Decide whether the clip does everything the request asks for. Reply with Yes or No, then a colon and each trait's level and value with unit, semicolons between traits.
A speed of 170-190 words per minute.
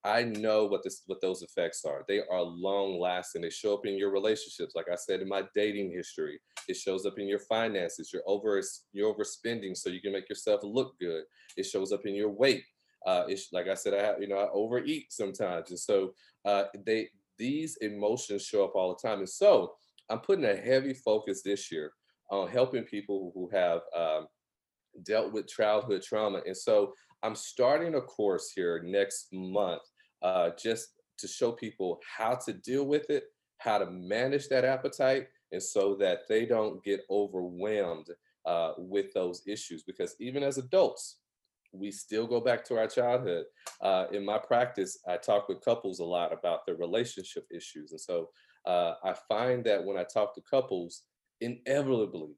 Yes: average, 185 wpm